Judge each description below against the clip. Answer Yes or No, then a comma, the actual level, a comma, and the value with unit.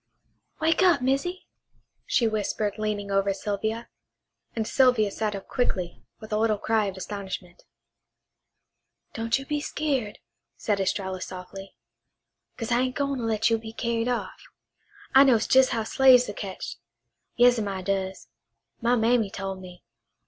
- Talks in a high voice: Yes, high, 220 Hz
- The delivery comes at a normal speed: Yes, average, 150 wpm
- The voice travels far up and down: No, average, 3.9 semitones